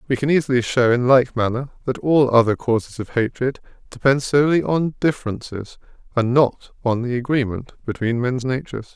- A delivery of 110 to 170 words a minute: Yes, average, 165 wpm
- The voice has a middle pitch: No, low, 125 Hz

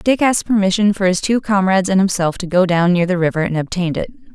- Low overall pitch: No, high, 190 Hz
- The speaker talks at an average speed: No, fast, 250 wpm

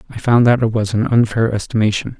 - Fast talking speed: Yes, fast, 220 wpm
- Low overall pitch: Yes, low, 110 Hz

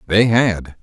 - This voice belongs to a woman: No, male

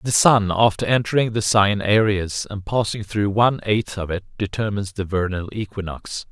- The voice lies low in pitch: Yes, low, 105 Hz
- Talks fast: No, average, 170 wpm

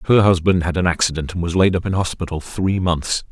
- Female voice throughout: No, male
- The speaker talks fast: Yes, fast, 235 wpm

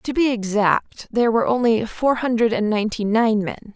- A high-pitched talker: Yes, high, 225 Hz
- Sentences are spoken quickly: No, average, 190 wpm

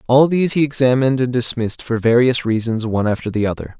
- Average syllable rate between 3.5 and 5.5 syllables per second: No, 6.6 syllables/s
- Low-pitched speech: Yes, low, 125 Hz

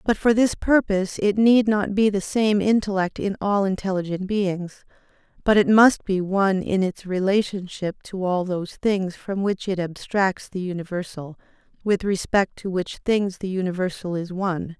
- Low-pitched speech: No, high, 195 Hz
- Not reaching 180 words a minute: Yes, average, 170 wpm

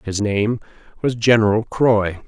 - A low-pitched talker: Yes, low, 110 Hz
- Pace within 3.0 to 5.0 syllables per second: Yes, 4.1 syllables/s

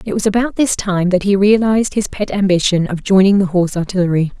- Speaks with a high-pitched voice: Yes, high, 195 Hz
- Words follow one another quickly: Yes, fast, 220 wpm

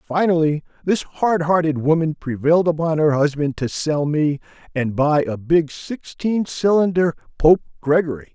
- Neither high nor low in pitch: Yes, medium, 160 Hz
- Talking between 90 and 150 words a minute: Yes, average, 145 wpm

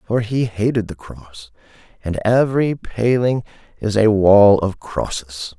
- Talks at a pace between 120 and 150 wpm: Yes, average, 140 wpm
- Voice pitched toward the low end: Yes, low, 110 Hz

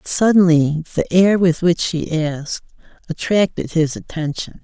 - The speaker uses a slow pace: Yes, slow, 130 wpm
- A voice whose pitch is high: No, medium, 170 Hz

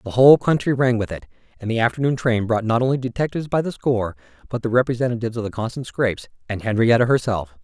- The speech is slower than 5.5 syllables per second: No, 7.0 syllables/s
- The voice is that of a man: Yes, male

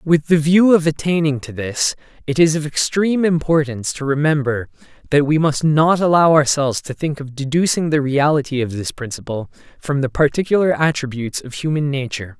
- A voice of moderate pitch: Yes, medium, 150 Hz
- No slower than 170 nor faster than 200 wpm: Yes, average, 175 wpm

